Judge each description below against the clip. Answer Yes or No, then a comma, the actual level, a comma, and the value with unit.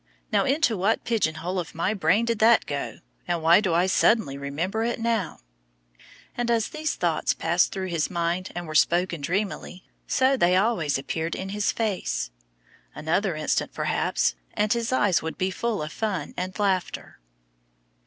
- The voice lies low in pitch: No, medium, 185 Hz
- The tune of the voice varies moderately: Yes, average, 4.9 semitones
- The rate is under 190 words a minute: Yes, average, 170 wpm